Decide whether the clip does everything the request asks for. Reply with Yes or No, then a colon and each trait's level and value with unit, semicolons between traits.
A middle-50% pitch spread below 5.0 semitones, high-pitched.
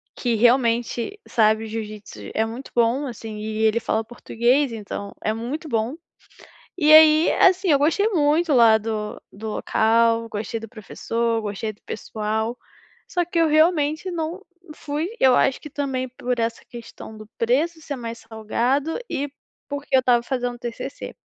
Yes: average, 4.6 semitones; high, 240 Hz